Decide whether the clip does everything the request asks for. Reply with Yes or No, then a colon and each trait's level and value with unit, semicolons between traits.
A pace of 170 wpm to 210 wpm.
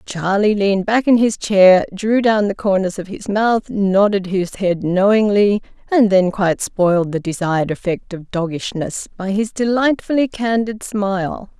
No: average, 160 wpm